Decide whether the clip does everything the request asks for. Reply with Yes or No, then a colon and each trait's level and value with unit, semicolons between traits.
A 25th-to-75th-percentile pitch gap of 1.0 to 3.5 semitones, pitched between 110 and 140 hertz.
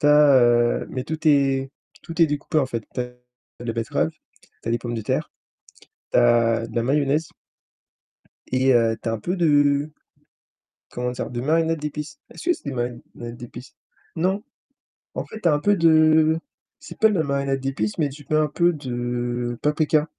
No: average, 4.1 semitones; low, 135 Hz